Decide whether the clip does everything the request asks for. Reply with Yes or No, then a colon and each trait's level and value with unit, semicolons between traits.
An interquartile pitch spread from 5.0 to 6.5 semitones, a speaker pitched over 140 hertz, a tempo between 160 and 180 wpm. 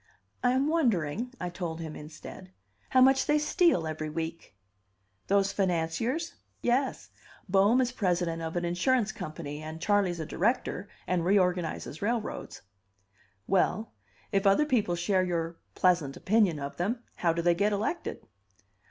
No: wide, 5.5 semitones; medium, 185 Hz; average, 145 wpm